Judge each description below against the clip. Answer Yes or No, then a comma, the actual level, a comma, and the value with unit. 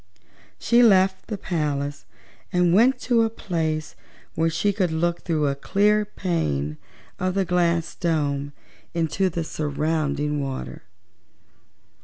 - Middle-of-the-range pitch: Yes, medium, 170 Hz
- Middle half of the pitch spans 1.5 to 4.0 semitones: No, average, 4.4 semitones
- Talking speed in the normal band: No, slow, 125 wpm